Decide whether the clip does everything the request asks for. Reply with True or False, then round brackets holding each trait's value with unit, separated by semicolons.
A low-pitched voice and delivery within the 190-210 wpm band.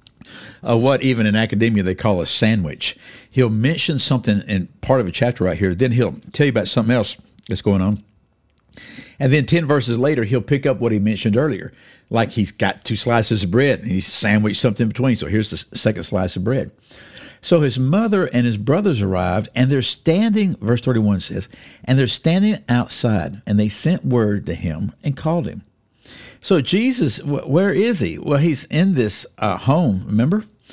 True (120 Hz; 195 wpm)